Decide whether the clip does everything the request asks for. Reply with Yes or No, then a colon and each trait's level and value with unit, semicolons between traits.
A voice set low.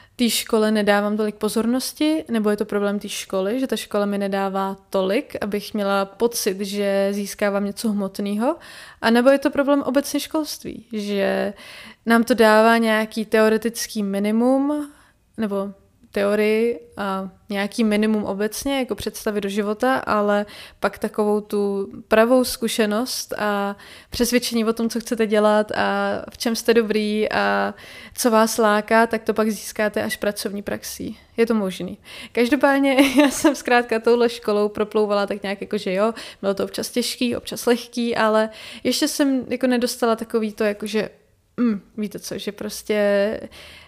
No: high, 220 Hz